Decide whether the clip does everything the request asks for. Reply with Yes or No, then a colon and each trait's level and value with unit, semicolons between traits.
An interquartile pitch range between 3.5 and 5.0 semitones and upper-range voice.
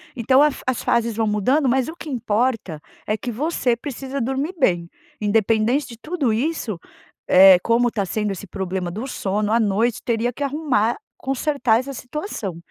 Yes: average, 4.2 semitones; high, 235 Hz